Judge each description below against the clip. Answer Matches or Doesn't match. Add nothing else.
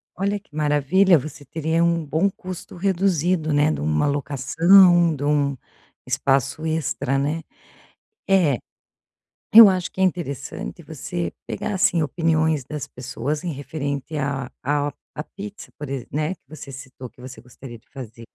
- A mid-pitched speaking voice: Matches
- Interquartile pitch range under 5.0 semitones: Matches